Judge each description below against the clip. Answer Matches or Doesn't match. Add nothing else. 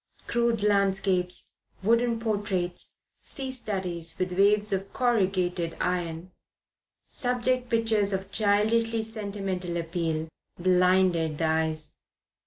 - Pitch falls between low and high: Doesn't match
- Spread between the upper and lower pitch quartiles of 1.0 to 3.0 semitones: Doesn't match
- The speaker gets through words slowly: Matches